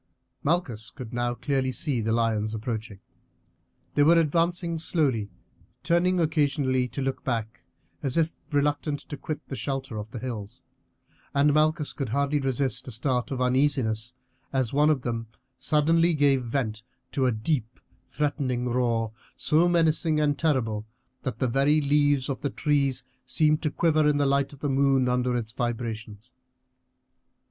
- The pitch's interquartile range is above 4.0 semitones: No, average, 3.7 semitones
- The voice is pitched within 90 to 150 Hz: Yes, low, 135 Hz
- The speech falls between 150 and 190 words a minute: Yes, average, 155 wpm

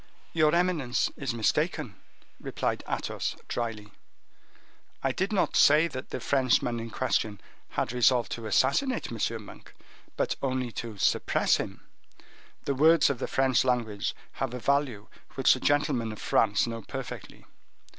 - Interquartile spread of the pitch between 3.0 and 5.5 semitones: Yes, average, 3.6 semitones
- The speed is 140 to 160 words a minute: Yes, average, 145 wpm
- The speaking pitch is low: Yes, low, 125 Hz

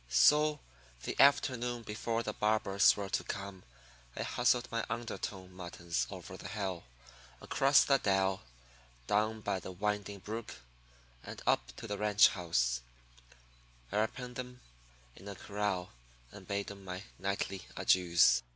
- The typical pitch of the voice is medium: No, low, 100 Hz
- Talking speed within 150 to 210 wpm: No, average, 140 wpm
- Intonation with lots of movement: No, average, 3.5 semitones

